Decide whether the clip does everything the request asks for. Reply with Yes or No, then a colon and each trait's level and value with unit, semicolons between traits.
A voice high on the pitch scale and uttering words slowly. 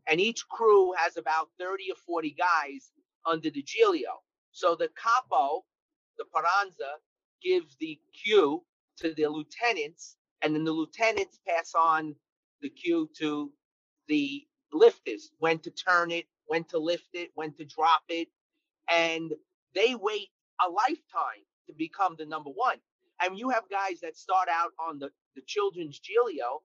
No: high, 200 Hz; average, 155 wpm